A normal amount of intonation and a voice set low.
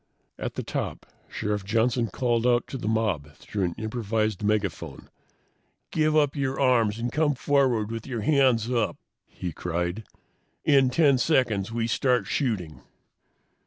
Yes: average, 3.9 semitones; low, 115 Hz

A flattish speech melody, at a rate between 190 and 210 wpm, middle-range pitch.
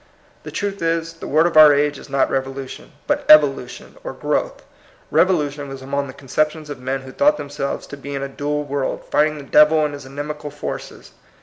Yes: narrow, 1.9 semitones; fast, 205 wpm; medium, 145 Hz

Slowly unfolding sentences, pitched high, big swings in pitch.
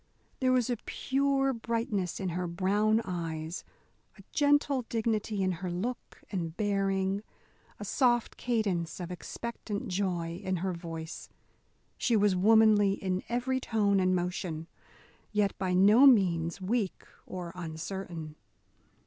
No: slow, 130 wpm; high, 195 Hz; average, 4.1 semitones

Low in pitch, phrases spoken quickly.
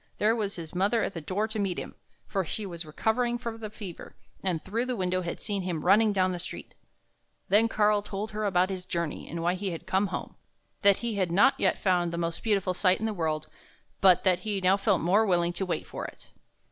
No: high, 190 Hz; fast, 235 wpm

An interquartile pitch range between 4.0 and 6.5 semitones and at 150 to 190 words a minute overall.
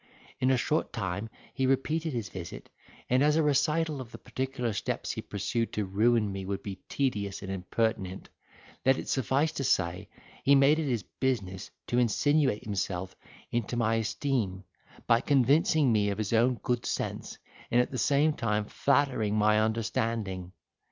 Yes: average, 4.8 semitones; average, 165 wpm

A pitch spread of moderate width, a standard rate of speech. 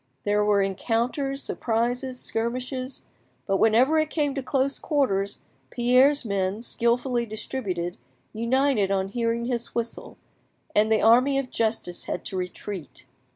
No: average, 3.9 semitones; slow, 130 wpm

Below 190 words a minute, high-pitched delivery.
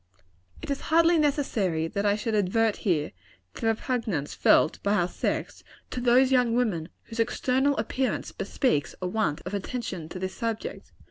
Yes: average, 170 wpm; high, 225 Hz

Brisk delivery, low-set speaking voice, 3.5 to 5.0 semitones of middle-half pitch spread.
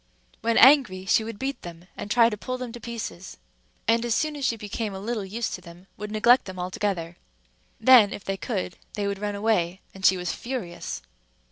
No: fast, 210 wpm; high, 210 Hz; average, 3.8 semitones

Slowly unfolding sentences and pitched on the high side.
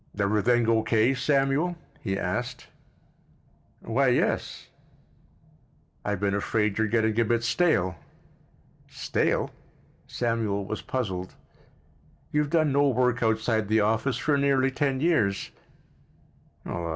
No: slow, 110 wpm; low, 115 Hz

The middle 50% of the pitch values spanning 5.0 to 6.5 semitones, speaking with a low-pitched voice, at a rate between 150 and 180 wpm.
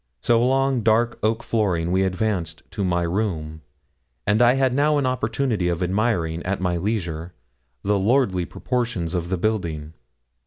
Yes: average, 5.3 semitones; low, 100 Hz; average, 155 wpm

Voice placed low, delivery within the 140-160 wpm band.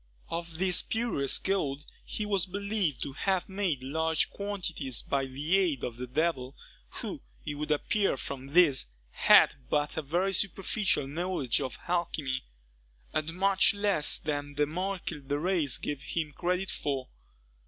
No: medium, 160 Hz; average, 150 wpm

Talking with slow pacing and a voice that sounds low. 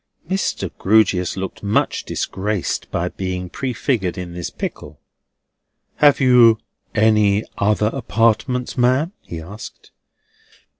Yes: slow, 105 wpm; low, 105 Hz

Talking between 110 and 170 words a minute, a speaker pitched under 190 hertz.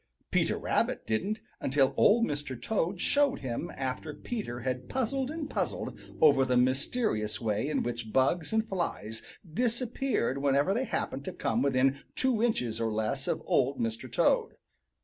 Yes: average, 155 wpm; medium, 140 Hz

